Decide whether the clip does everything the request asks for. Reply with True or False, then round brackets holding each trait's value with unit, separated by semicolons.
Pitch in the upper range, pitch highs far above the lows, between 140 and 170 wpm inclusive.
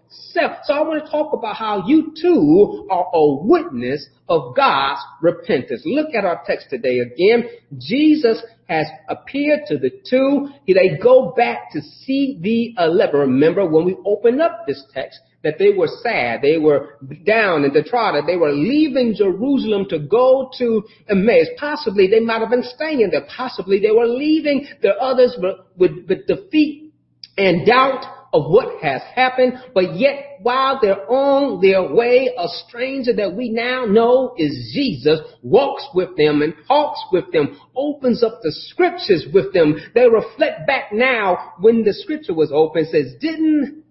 True (250 Hz; 7.5 semitones; 165 wpm)